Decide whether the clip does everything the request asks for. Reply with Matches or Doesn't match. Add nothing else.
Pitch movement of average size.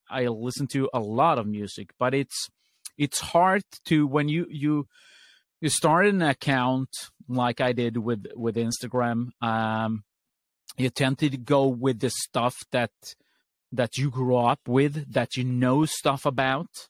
Matches